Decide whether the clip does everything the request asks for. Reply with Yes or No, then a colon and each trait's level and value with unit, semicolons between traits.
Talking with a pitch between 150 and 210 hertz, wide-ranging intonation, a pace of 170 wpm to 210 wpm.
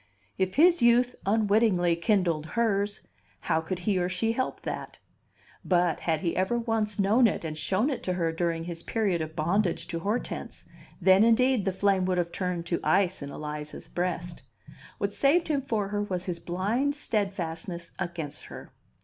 No: medium, 185 Hz; average, 4.4 semitones; average, 175 wpm